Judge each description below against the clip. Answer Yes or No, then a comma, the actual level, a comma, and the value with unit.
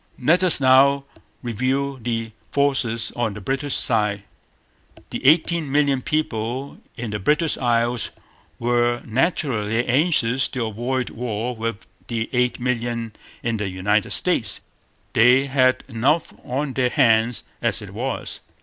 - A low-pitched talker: Yes, low, 125 Hz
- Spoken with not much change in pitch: No, average, 3.1 semitones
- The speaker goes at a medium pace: No, slow, 130 wpm